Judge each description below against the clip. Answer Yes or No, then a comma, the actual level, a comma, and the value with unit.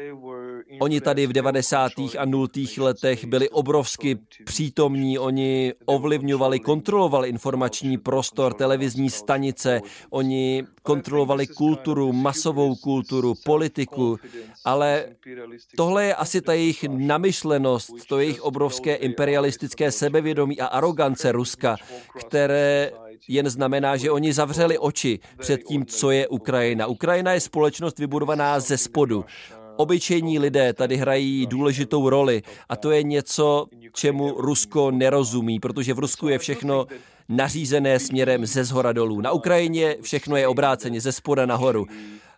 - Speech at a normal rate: Yes, average, 125 wpm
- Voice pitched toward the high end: No, low, 135 Hz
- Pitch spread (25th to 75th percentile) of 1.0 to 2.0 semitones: No, narrow, 2.4 semitones